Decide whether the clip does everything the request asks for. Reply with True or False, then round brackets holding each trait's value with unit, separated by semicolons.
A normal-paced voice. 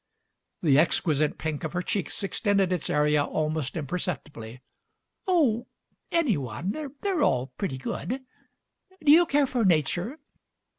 False (130 wpm)